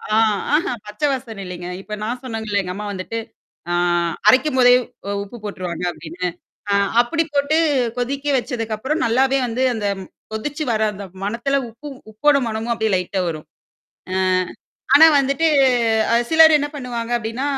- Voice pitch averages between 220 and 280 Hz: Yes, high, 230 Hz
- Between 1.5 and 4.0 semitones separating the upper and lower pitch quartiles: No, average, 4.7 semitones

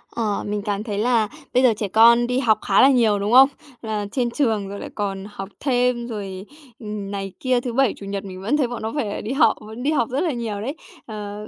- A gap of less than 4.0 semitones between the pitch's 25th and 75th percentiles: Yes, average, 3.3 semitones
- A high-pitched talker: Yes, high, 220 Hz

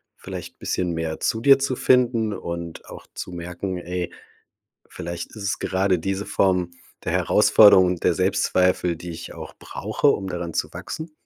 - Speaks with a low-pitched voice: Yes, very low, 90 Hz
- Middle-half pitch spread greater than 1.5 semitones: Yes, average, 2.8 semitones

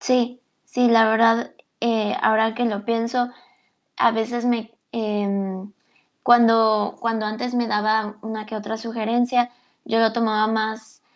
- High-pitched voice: Yes, high, 225 Hz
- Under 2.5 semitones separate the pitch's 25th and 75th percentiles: Yes, narrow, 1.5 semitones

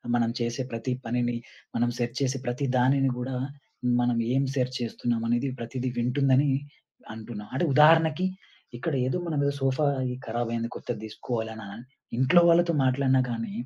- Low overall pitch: Yes, low, 125 Hz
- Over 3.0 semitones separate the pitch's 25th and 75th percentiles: No, narrow, 2.6 semitones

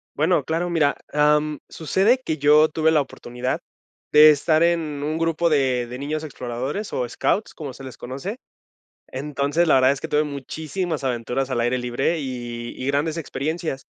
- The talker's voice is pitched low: No, medium, 145 Hz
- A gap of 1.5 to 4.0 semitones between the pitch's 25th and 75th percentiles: Yes, average, 3.4 semitones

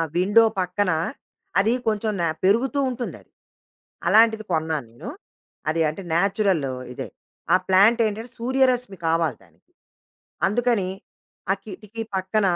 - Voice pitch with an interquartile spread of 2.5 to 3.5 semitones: No, average, 4.0 semitones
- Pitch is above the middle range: Yes, high, 205 Hz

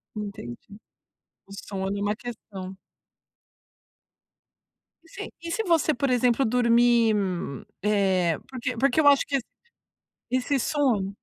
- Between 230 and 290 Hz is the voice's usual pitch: Yes, high, 235 Hz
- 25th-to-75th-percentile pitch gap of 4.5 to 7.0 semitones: Yes, average, 4.9 semitones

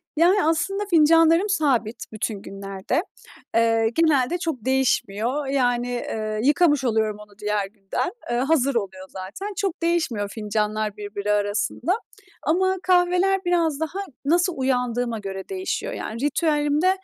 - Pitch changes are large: Yes, wide, 7.6 semitones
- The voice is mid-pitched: No, very high, 260 Hz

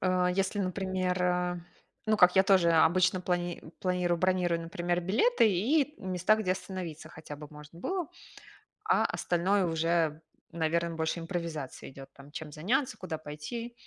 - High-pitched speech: No, medium, 180 Hz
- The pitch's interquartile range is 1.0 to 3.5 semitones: Yes, narrow, 2.4 semitones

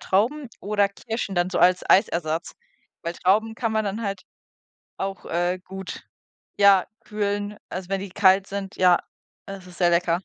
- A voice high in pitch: Yes, high, 195 Hz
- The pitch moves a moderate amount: No, narrow, 2.2 semitones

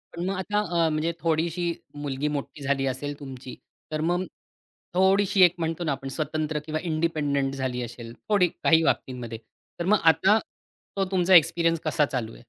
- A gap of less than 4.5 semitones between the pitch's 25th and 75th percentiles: Yes, average, 3.9 semitones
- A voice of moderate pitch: Yes, medium, 160 Hz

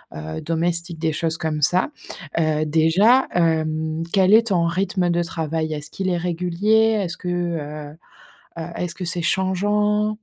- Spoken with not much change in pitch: No, average, 3.0 semitones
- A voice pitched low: No, medium, 170 Hz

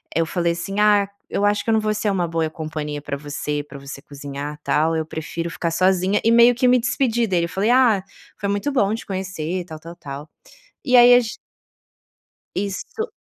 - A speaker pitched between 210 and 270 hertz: No, medium, 185 Hz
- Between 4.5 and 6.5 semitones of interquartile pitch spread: Yes, wide, 5.4 semitones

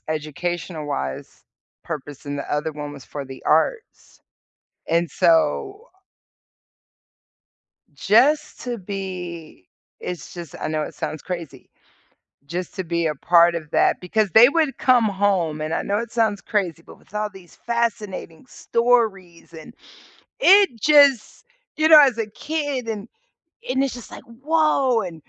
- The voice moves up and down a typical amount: No, wide, 7.0 semitones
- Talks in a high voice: Yes, high, 195 Hz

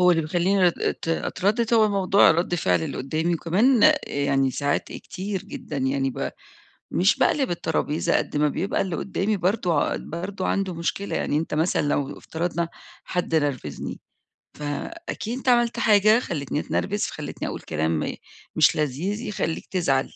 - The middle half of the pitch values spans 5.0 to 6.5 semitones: Yes, wide, 5.4 semitones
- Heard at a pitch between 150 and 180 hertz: Yes, medium, 175 Hz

